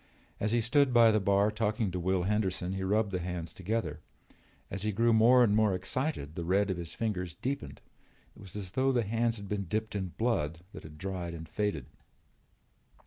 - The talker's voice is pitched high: No, low, 100 Hz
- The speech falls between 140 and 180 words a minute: No, average, 200 wpm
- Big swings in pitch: No, average, 3.6 semitones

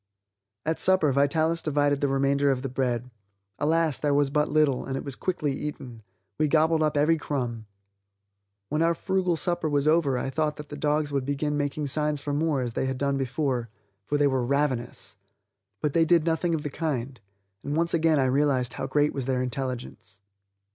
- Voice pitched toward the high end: No, medium, 145 Hz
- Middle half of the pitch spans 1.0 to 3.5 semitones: Yes, narrow, 2.5 semitones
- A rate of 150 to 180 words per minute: No, average, 195 wpm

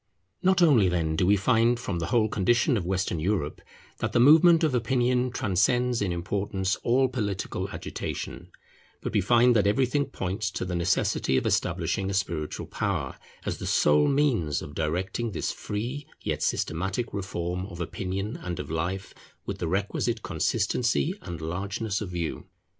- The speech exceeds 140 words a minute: Yes, average, 165 wpm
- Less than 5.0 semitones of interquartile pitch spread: No, wide, 5.4 semitones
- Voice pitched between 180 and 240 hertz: No, low, 100 Hz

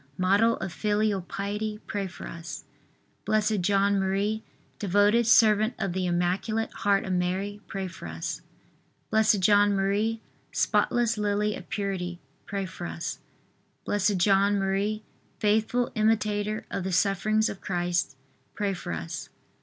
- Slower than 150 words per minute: Yes, slow, 135 wpm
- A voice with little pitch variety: Yes, narrow, 2.1 semitones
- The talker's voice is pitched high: Yes, high, 200 Hz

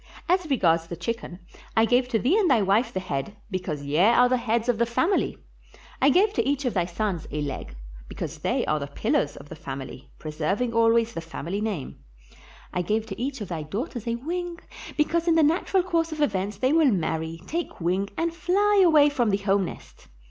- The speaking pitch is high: Yes, high, 225 Hz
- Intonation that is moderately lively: No, wide, 8.8 semitones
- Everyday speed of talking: No, fast, 210 wpm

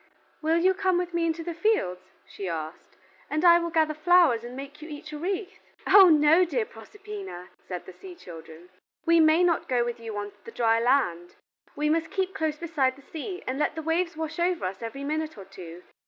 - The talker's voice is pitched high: Yes, very high, 310 Hz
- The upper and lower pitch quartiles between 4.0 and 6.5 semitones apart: No, wide, 6.9 semitones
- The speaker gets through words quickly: Yes, fast, 215 wpm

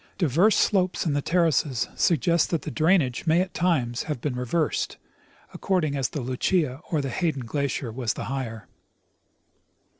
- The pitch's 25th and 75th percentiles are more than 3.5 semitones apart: Yes, average, 5.1 semitones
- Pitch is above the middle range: No, medium, 150 Hz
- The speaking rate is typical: Yes, average, 160 wpm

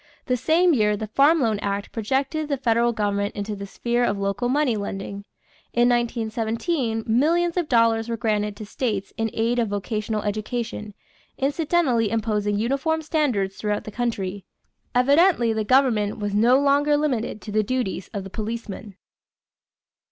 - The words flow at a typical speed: Yes, average, 155 wpm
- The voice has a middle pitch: No, high, 225 Hz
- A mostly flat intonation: No, average, 4.1 semitones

